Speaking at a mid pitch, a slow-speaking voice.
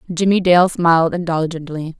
Yes: medium, 170 Hz; slow, 120 wpm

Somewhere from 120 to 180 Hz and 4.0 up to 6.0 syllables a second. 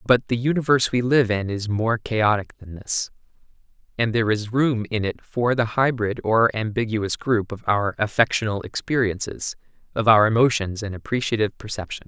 No: low, 110 Hz; 5.1 syllables/s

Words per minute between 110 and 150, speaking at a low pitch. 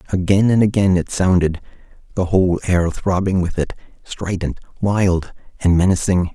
Yes: average, 140 wpm; very low, 90 Hz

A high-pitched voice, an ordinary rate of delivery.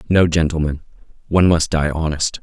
No: very low, 80 Hz; average, 150 wpm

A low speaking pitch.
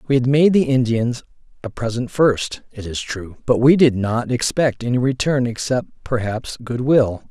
Yes: low, 125 Hz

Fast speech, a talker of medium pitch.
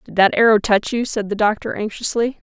No: fast, 215 wpm; high, 215 Hz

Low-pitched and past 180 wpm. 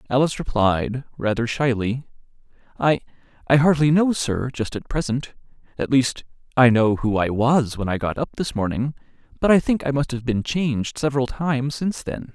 No: low, 130 Hz; average, 170 wpm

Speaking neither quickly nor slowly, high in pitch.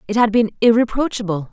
Yes: average, 160 wpm; high, 220 Hz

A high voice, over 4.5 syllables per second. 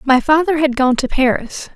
Yes: very high, 275 Hz; 4.9 syllables/s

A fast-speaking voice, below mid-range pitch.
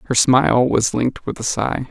Yes: fast, 220 wpm; low, 120 Hz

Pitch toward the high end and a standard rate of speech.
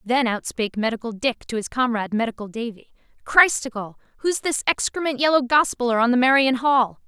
Yes: high, 245 Hz; average, 160 wpm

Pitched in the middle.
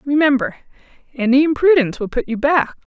No: very high, 270 Hz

